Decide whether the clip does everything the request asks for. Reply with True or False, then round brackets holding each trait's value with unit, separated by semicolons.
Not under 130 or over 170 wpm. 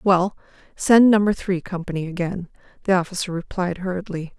True (135 wpm)